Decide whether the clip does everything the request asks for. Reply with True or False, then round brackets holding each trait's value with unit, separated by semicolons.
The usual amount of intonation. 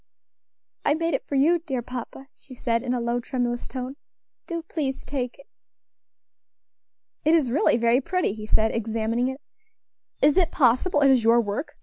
True (3.7 semitones)